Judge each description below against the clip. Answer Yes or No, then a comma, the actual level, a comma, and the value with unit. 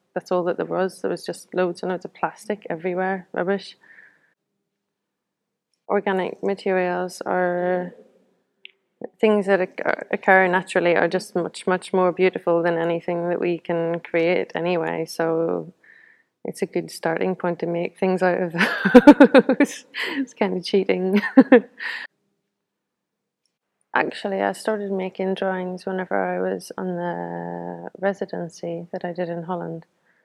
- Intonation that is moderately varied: No, narrow, 2.3 semitones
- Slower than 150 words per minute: Yes, slow, 135 wpm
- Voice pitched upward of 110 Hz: Yes, medium, 185 Hz